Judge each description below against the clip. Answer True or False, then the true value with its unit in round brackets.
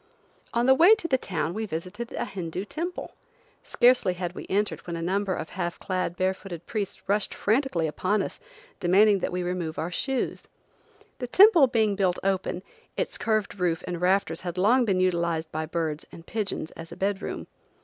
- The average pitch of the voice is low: False (190 Hz)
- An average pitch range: True (3.9 semitones)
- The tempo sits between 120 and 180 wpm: False (190 wpm)